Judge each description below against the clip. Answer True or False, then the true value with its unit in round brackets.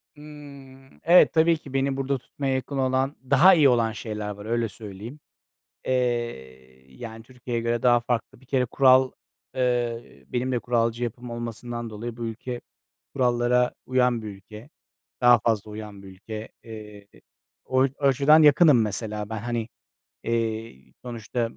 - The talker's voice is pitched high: False (120 Hz)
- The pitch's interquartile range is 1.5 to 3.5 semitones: True (2.9 semitones)